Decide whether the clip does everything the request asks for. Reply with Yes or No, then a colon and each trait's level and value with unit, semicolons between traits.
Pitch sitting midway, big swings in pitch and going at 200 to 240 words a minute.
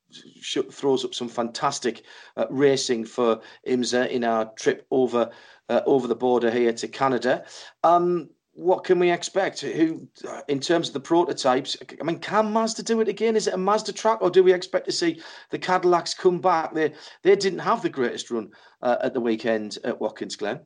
No: medium, 170 Hz; wide, 8.4 semitones; average, 190 wpm